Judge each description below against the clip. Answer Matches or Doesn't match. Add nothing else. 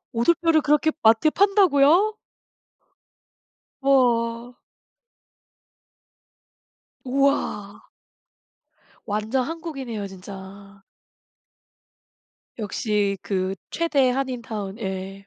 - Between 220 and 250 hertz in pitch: Matches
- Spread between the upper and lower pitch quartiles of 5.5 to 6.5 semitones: Matches